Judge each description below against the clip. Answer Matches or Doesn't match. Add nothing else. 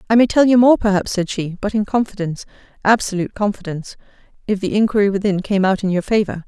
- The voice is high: Matches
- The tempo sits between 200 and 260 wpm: Matches